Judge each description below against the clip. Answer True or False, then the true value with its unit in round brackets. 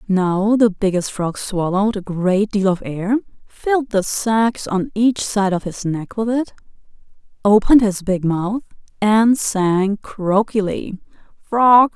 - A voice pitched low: False (205 Hz)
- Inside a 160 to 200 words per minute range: False (145 wpm)